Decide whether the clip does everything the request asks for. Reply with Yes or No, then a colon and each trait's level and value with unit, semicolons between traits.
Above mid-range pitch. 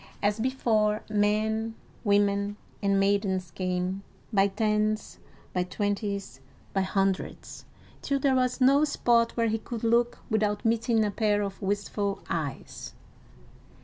Yes: high, 210 Hz